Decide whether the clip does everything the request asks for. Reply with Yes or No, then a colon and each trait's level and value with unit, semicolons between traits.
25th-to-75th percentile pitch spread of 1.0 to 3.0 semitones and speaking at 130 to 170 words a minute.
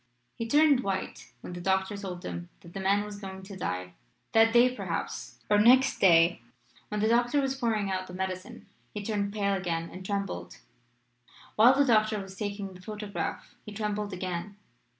No: average, 2.7 semitones; average, 180 wpm